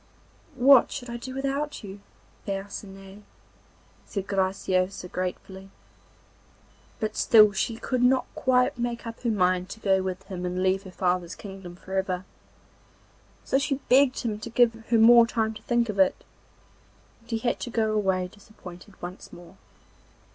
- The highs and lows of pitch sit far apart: No, average, 4.0 semitones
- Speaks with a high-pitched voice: Yes, high, 205 Hz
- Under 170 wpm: Yes, average, 155 wpm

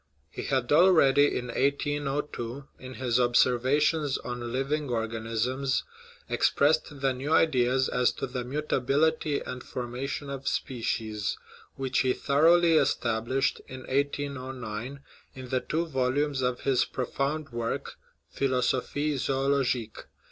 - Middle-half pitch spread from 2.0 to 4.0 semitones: Yes, narrow, 2.4 semitones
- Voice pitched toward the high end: No, low, 130 Hz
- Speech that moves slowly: Yes, slow, 120 wpm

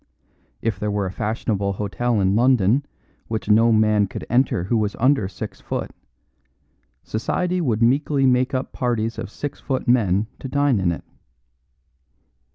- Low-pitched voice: Yes, low, 115 Hz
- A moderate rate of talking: Yes, average, 155 wpm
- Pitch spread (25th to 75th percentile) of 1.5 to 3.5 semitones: No, average, 3.9 semitones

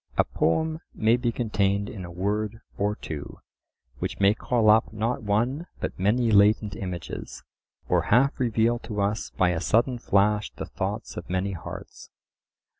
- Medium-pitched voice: No, low, 105 Hz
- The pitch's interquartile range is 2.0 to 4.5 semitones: Yes, average, 2.9 semitones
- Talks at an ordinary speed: Yes, average, 160 wpm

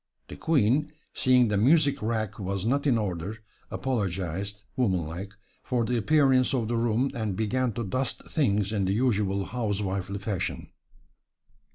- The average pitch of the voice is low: Yes, low, 110 Hz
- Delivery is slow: No, average, 145 wpm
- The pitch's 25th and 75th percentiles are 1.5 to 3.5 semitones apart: No, average, 4.4 semitones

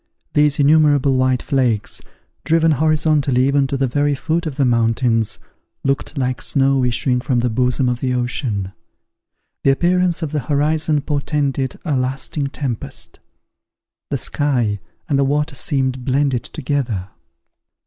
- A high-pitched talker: No, low, 135 Hz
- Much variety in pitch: No, average, 2.8 semitones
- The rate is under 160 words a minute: Yes, average, 140 wpm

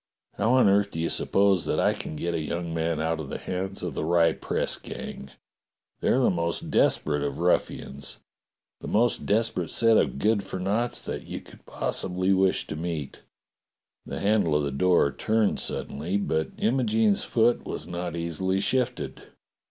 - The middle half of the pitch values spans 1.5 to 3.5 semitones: No, average, 4.1 semitones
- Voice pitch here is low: Yes, very low, 90 Hz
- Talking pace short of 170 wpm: No, average, 175 wpm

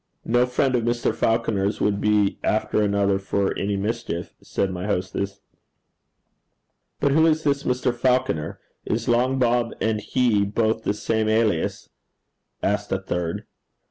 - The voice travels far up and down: No, average, 3.5 semitones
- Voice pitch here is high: No, low, 110 Hz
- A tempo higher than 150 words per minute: No, average, 140 wpm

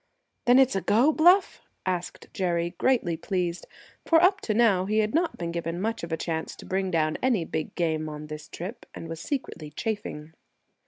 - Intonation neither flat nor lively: No, wide, 6.2 semitones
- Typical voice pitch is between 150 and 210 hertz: Yes, medium, 185 Hz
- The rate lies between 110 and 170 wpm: No, average, 195 wpm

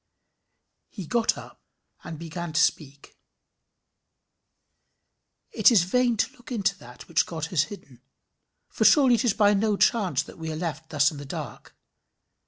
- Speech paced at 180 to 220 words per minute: No, average, 165 wpm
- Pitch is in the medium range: Yes, medium, 175 Hz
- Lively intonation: Yes, wide, 5.9 semitones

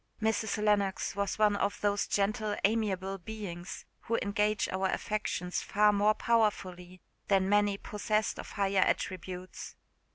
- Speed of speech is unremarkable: No, slow, 130 wpm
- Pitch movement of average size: No, narrow, 1.9 semitones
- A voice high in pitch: Yes, high, 205 Hz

